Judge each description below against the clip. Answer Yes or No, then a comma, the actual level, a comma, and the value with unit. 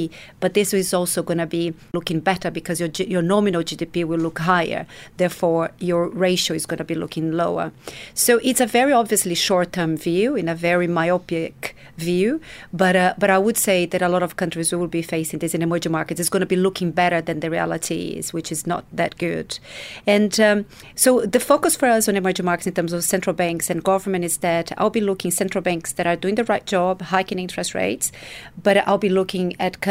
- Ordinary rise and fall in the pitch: No, narrow, 2.3 semitones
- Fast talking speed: Yes, fast, 225 wpm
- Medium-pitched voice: Yes, medium, 180 Hz